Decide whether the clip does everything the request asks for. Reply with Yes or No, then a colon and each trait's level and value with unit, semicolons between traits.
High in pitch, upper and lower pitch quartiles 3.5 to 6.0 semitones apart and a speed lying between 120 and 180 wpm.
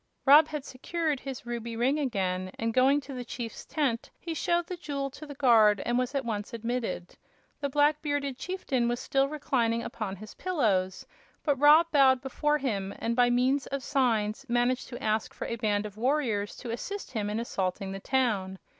No: very high, 250 Hz; average, 4.4 semitones; average, 190 wpm